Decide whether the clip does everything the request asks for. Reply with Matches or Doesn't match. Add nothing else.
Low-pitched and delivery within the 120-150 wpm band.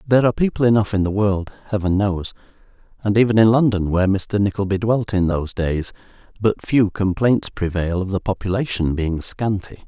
Doesn't match